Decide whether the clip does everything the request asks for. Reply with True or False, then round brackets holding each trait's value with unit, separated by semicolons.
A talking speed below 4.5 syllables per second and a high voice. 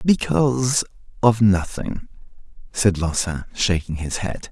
False (4.0 syllables/s; 105 Hz)